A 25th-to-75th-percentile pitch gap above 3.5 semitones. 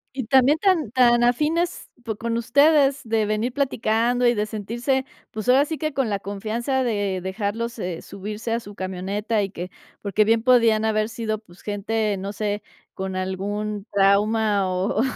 No: average, 3.1 semitones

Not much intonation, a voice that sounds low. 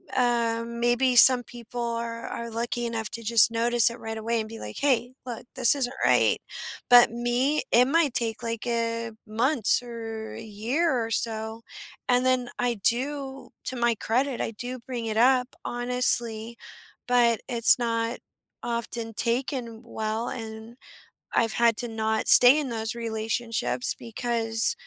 No: narrow, 1.4 semitones; high, 235 Hz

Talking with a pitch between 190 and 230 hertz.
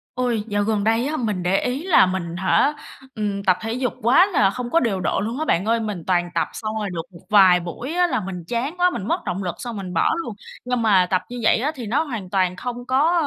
Yes: high, 220 Hz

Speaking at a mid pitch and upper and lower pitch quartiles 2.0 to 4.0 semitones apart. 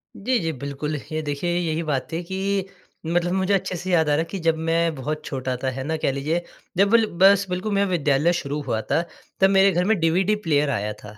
No: medium, 165 Hz; average, 4.6 semitones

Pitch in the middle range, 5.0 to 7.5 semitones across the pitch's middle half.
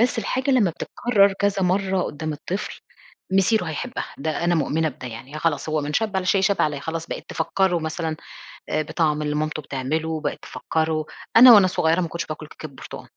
No: medium, 160 Hz; average, 4.0 semitones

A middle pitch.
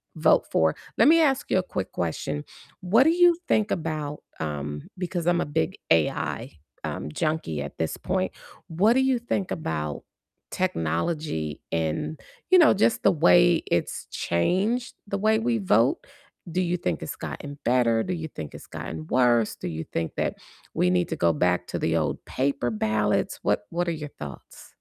Yes: medium, 150 Hz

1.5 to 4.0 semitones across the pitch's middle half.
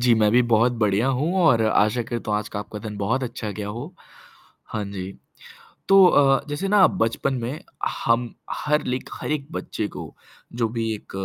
No: average, 4.5 semitones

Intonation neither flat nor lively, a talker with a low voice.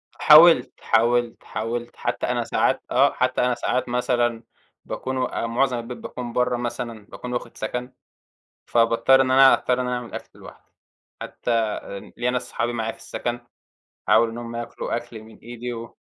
No: narrow, 1.1 semitones; low, 120 Hz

